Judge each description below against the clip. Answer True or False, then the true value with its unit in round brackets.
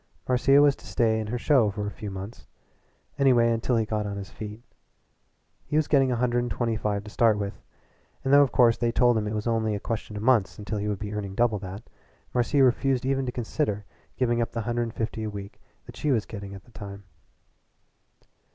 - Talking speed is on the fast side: True (225 wpm)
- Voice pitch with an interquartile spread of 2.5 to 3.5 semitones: True (2.8 semitones)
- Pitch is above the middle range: False (115 Hz)